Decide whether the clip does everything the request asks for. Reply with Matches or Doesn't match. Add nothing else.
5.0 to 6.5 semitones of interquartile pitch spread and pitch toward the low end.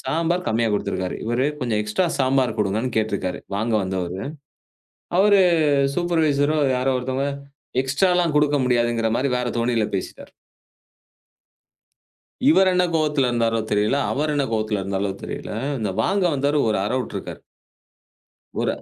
Matches